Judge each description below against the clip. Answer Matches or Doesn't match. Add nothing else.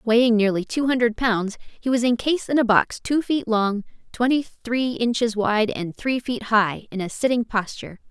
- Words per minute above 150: Matches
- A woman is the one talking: Matches